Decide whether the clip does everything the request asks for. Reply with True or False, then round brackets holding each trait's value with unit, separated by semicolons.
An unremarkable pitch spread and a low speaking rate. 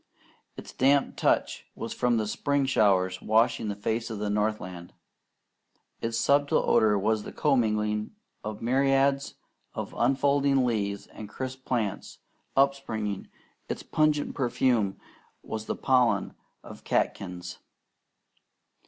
True (4.4 semitones; 120 wpm)